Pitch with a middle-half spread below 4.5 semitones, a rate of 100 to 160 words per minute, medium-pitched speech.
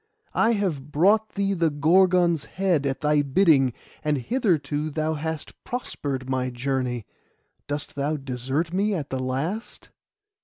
No: average, 5.1 semitones; average, 140 wpm; medium, 150 Hz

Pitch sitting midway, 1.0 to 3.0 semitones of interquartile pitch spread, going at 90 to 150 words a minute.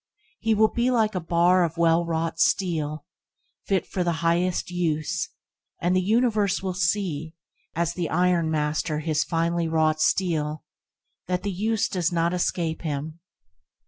Yes: medium, 170 Hz; narrow, 2.5 semitones; average, 145 wpm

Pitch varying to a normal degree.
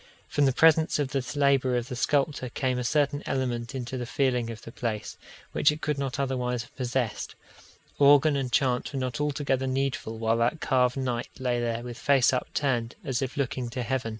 No: narrow, 2.3 semitones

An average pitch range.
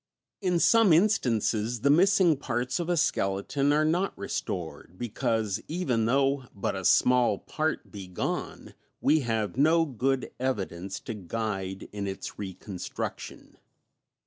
No: wide, 7.1 semitones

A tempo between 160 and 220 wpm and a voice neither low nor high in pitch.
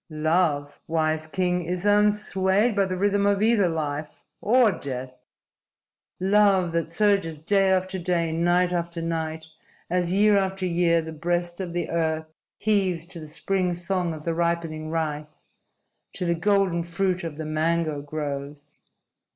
No: average, 150 wpm; medium, 170 Hz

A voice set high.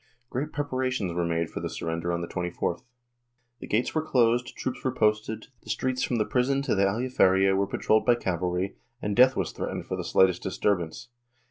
No: low, 105 Hz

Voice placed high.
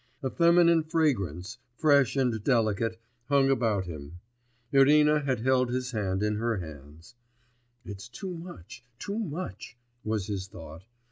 No: low, 120 Hz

